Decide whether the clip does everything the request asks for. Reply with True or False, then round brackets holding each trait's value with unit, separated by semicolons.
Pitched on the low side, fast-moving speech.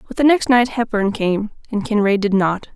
False (215 Hz; 220 wpm)